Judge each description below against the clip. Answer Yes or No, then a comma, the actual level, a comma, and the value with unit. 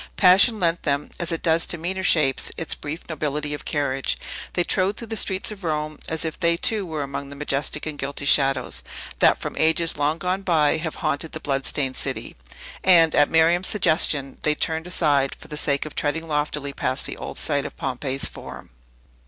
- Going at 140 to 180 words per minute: No, average, 200 wpm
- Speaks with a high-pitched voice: No, medium, 155 Hz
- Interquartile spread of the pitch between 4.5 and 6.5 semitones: No, average, 2.9 semitones